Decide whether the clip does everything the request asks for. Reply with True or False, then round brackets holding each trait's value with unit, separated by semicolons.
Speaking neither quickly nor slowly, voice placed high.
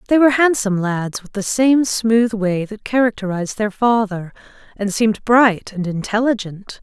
True (160 wpm; 215 Hz)